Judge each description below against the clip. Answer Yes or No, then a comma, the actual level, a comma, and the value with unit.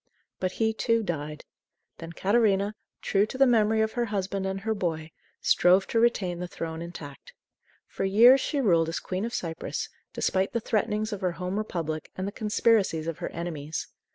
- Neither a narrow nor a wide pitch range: Yes, average, 4.5 semitones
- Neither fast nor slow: Yes, average, 180 wpm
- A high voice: Yes, high, 195 Hz